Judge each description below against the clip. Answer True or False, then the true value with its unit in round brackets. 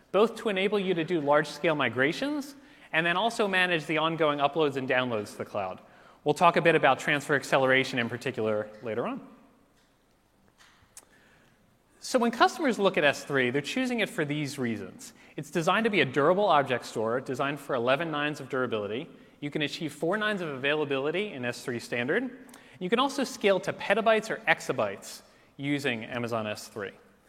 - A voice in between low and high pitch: True (155 Hz)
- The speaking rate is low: False (175 wpm)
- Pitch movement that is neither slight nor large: False (7.9 semitones)